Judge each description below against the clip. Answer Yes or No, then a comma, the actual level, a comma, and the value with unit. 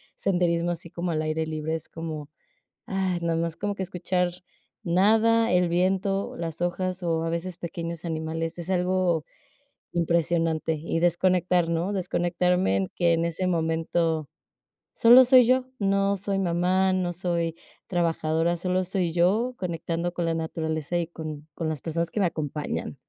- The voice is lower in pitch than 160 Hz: No, medium, 170 Hz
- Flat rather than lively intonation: Yes, narrow, 2.1 semitones